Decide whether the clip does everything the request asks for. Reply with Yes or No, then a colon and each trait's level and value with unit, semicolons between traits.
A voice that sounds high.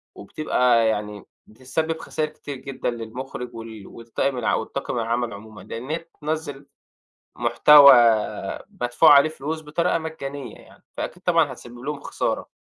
No: low, 135 Hz